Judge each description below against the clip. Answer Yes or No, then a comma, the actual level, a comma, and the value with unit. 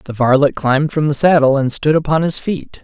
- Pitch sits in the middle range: Yes, medium, 145 Hz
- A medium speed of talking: No, fast, 235 wpm